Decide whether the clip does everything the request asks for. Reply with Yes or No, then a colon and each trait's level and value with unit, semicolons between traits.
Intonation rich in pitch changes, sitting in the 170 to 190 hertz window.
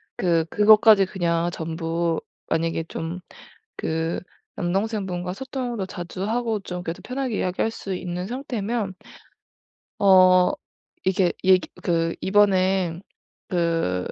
No: average, 3.5 semitones; medium, 185 Hz